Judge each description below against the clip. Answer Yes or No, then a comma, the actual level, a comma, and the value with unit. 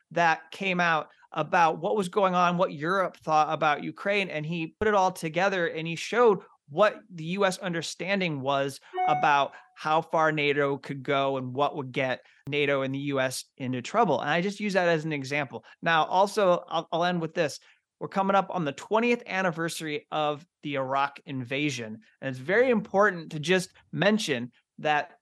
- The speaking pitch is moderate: Yes, medium, 165 Hz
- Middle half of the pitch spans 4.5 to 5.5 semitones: Yes, average, 4.8 semitones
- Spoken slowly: No, average, 185 wpm